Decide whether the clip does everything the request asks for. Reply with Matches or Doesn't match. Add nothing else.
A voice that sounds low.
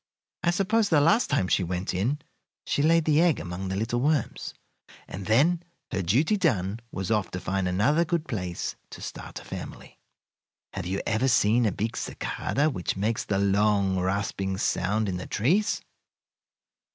Matches